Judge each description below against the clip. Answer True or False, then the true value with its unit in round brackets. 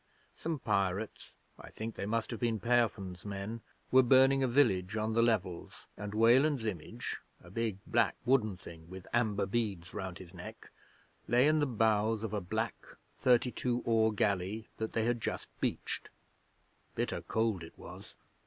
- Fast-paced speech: False (165 wpm)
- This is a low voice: True (110 Hz)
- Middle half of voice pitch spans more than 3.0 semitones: True (3.4 semitones)